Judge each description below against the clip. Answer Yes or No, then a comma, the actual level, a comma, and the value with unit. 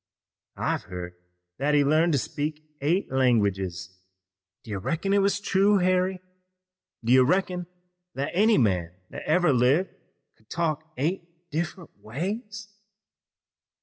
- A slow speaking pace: Yes, slow, 130 wpm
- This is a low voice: No, medium, 155 Hz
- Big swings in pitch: Yes, wide, 6.6 semitones